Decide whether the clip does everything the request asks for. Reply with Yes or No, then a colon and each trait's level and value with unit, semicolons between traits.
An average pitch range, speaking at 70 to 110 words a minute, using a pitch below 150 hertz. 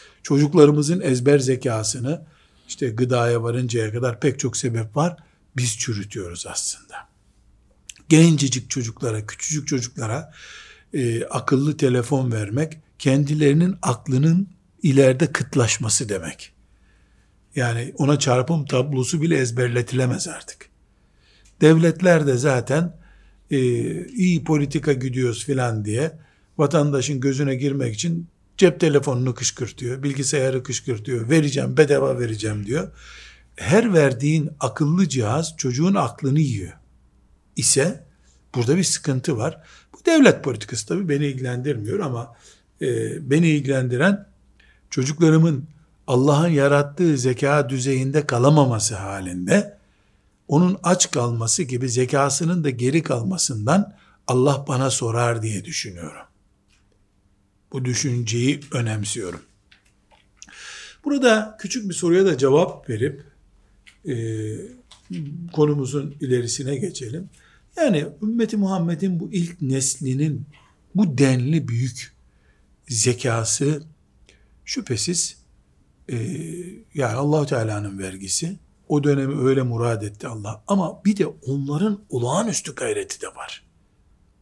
Yes: average, 4.8 semitones; average, 100 wpm; medium, 140 Hz